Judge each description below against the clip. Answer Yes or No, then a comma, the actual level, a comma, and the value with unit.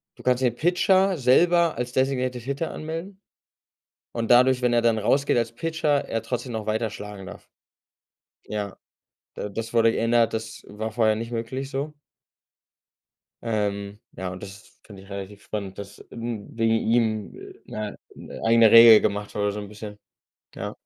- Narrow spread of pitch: No, average, 3.4 semitones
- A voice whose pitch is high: No, low, 115 Hz